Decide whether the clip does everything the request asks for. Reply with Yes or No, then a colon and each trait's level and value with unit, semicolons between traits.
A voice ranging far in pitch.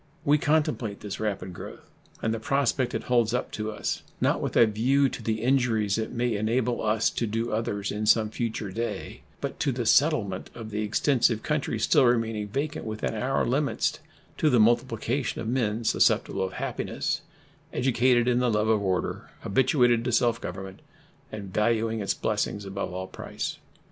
No: average, 2.7 semitones